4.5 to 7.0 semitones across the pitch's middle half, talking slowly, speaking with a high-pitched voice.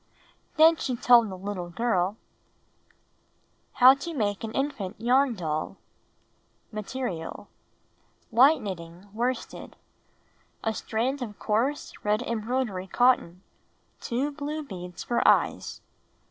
Yes: average, 5.0 semitones; slow, 120 wpm; high, 230 Hz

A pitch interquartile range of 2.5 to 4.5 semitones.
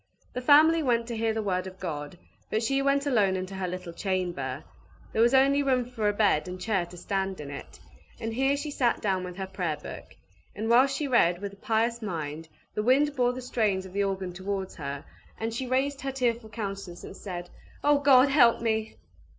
No: wide, 5.4 semitones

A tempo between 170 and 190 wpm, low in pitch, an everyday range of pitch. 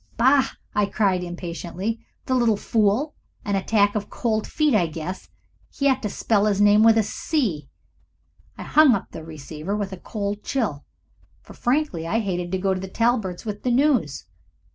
No: average, 180 wpm; high, 205 Hz; average, 4.2 semitones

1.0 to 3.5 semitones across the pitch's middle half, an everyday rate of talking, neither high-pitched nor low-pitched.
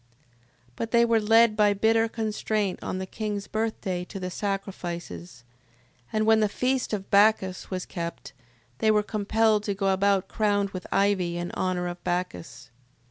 No: average, 2.9 semitones; average, 165 wpm; high, 200 Hz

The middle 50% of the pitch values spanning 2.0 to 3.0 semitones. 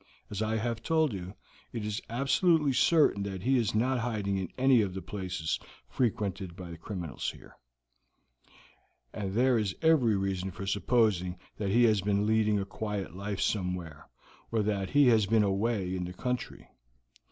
No: average, 3.6 semitones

